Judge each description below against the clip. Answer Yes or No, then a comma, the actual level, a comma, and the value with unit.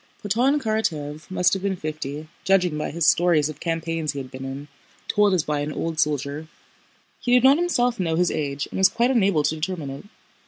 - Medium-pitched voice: Yes, medium, 165 Hz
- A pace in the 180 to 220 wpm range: Yes, fast, 205 wpm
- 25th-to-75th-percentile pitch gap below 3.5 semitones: No, average, 4.8 semitones